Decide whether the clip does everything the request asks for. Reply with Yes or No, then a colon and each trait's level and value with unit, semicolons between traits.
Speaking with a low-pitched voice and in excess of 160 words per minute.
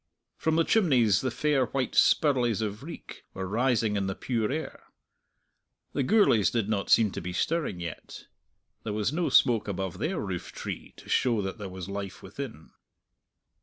Yes: low, 115 Hz; average, 170 wpm